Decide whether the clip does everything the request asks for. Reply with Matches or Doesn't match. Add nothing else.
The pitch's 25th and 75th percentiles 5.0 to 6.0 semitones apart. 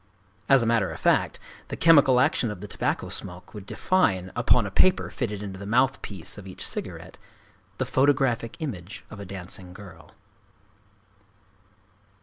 Matches